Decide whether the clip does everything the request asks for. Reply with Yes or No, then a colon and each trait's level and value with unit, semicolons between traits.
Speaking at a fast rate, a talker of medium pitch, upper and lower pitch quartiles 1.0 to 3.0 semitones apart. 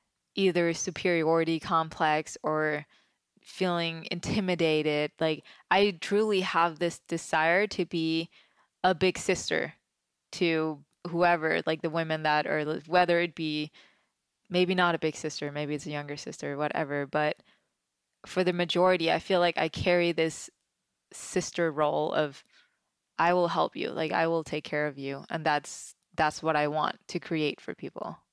No: average, 155 wpm; medium, 165 Hz; narrow, 2.5 semitones